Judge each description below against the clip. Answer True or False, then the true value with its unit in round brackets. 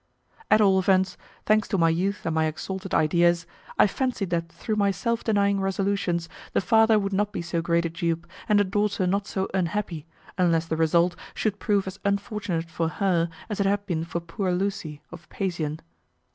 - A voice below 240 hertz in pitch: True (190 Hz)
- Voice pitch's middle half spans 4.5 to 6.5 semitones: False (3.2 semitones)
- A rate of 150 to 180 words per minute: False (190 wpm)